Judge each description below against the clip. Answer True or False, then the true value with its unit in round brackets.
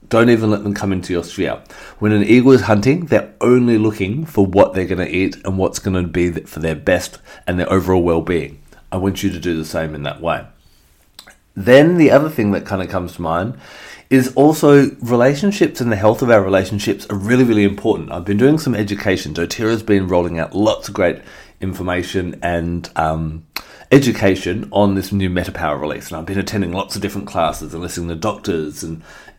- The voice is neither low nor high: False (95 Hz)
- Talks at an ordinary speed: False (210 wpm)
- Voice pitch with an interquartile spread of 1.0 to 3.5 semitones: False (3.9 semitones)